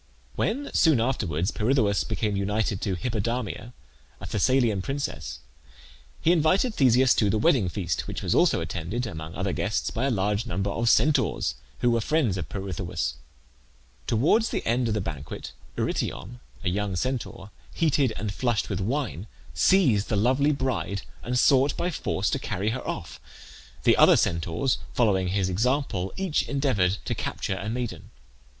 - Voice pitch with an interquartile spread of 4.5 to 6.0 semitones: Yes, wide, 5.4 semitones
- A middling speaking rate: Yes, average, 155 wpm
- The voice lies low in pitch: Yes, low, 110 Hz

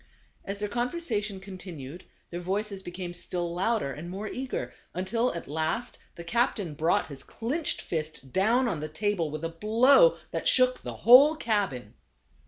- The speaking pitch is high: Yes, high, 195 Hz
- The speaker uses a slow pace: No, average, 165 wpm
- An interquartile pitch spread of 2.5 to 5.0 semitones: No, wide, 5.6 semitones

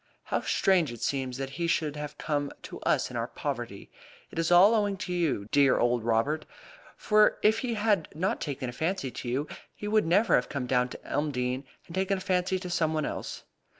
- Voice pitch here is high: No, medium, 155 Hz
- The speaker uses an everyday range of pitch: No, wide, 6.0 semitones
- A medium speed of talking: No, fast, 215 wpm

